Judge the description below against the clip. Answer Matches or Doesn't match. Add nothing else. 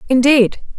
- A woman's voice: Matches